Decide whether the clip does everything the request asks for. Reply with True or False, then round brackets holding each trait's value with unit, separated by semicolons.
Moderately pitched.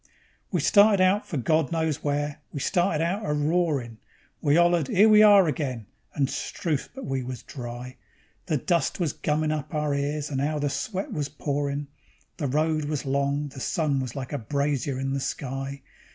True (145 Hz)